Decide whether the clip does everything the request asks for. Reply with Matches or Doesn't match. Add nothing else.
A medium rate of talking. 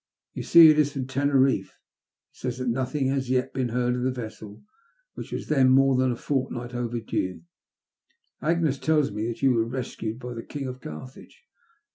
Matches